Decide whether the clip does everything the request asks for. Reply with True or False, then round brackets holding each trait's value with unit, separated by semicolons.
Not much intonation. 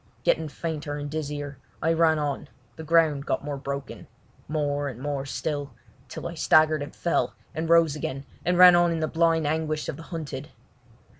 True (2.2 semitones)